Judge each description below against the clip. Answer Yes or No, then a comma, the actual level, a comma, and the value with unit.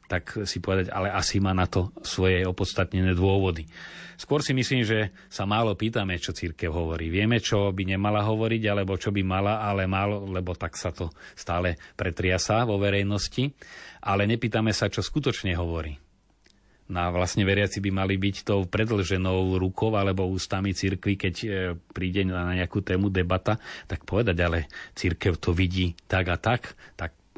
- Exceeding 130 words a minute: Yes, fast, 165 wpm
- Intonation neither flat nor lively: No, narrow, 2.2 semitones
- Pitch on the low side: Yes, very low, 95 Hz